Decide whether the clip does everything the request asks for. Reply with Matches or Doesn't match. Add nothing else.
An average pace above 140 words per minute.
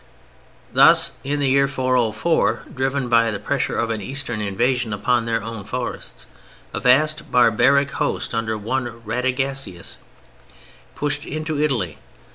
Doesn't match